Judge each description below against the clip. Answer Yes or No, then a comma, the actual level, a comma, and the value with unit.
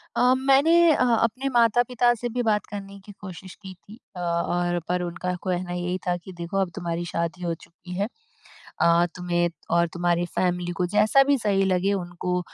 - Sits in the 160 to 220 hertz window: Yes, medium, 185 Hz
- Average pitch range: Yes, average, 3.7 semitones